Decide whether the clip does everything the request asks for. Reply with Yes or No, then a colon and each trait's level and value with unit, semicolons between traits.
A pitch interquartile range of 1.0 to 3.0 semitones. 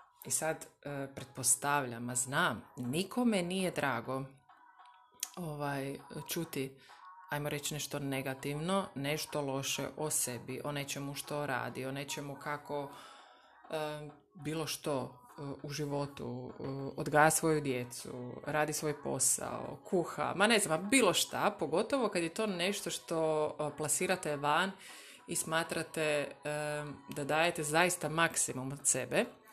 Yes: average, 2.7 semitones